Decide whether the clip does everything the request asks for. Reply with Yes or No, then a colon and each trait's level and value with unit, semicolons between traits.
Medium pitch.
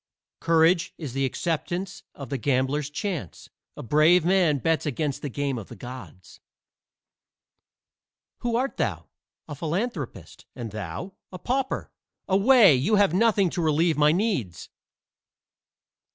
Yes: medium, 160 Hz